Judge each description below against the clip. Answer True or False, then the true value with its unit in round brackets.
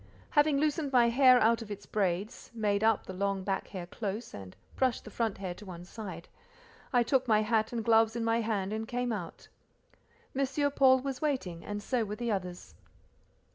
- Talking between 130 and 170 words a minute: False (195 wpm)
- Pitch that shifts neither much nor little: True (4.0 semitones)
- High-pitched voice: True (220 Hz)